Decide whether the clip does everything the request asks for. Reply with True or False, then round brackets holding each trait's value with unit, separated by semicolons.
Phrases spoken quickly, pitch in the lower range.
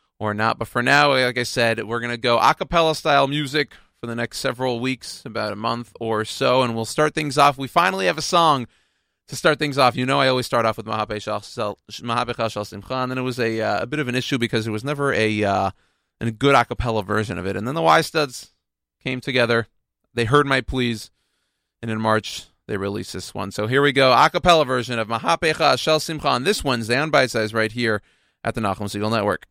True (225 wpm; 120 Hz)